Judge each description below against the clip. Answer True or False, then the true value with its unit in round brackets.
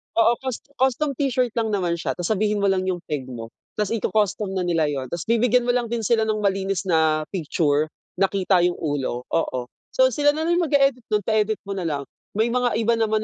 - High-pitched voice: True (205 Hz)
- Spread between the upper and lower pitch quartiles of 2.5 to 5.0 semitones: False (5.5 semitones)